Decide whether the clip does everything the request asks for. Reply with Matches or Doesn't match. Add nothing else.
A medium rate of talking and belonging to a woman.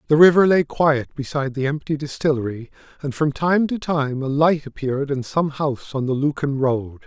Doesn't match